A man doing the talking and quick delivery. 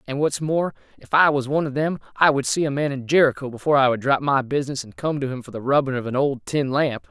Yes: male; fast, 285 wpm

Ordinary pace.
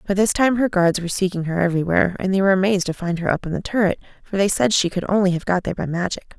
No: fast, 290 wpm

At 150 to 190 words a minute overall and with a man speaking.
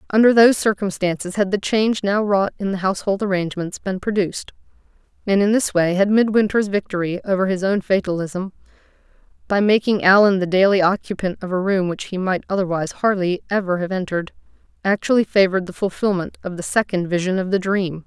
No: average, 170 wpm; female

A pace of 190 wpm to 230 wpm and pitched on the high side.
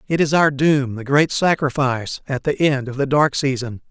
No: average, 200 wpm; medium, 140 Hz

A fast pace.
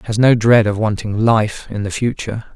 Yes: fast, 210 wpm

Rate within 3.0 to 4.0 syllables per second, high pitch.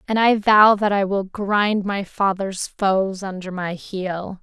Yes: 3.6 syllables/s; high, 195 Hz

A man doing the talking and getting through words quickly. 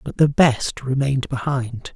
No: male; average, 155 wpm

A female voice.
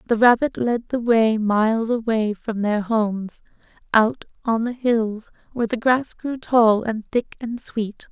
Yes: female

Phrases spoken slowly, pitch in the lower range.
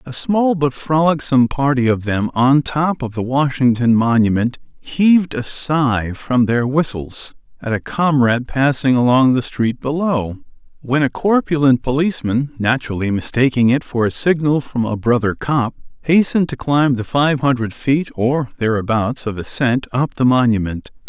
No: average, 155 wpm; low, 130 Hz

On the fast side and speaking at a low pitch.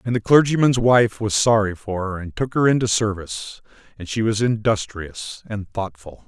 No: average, 180 wpm; low, 110 Hz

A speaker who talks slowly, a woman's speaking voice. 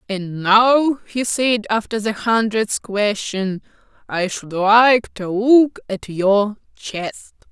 Yes: slow, 130 wpm; female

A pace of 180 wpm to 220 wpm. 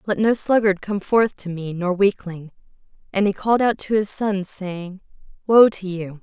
Yes: average, 195 wpm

